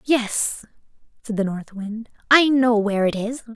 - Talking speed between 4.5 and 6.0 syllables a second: No, 4.2 syllables/s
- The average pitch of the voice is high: Yes, high, 225 Hz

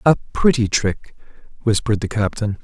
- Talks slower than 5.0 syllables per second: No, 5.3 syllables/s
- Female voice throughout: No, male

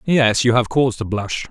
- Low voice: Yes, low, 120 Hz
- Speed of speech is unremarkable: No, fast, 240 wpm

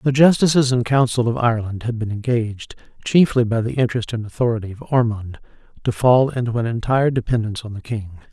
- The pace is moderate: Yes, average, 190 wpm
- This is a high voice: No, low, 120 Hz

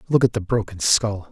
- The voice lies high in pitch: No, low, 110 Hz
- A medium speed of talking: No, fast, 230 wpm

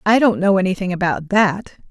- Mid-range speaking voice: No, high, 195 Hz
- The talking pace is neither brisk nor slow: Yes, average, 190 wpm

